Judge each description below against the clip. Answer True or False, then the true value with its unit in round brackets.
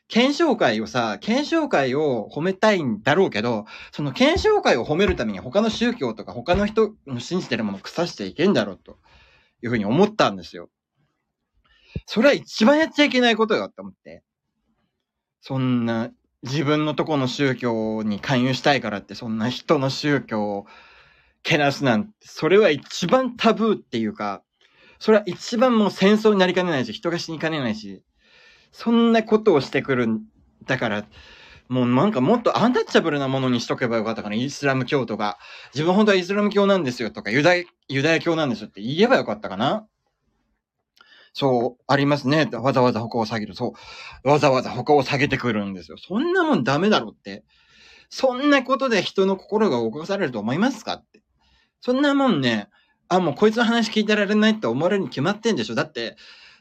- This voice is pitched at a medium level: True (155 Hz)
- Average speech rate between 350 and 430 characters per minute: True (385 characters per minute)